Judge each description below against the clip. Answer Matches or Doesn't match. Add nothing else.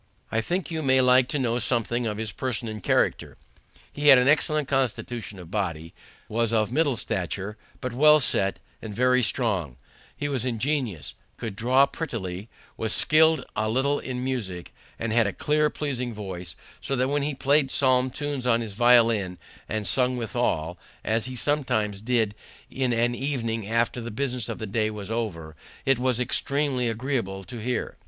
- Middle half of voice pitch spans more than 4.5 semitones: Doesn't match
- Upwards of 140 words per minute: Matches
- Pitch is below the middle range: Matches